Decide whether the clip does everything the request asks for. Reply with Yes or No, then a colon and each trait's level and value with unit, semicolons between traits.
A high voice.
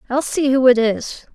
Yes: very high, 255 Hz